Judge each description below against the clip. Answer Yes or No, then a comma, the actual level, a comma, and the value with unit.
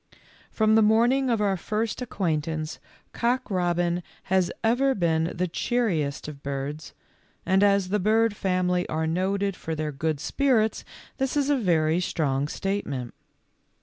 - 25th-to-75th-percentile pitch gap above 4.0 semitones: Yes, wide, 5.5 semitones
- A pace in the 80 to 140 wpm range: No, average, 150 wpm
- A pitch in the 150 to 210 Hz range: Yes, medium, 185 Hz